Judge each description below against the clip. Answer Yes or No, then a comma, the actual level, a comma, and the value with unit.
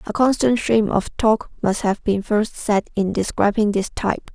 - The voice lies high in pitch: Yes, high, 210 Hz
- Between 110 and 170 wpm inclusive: No, average, 195 wpm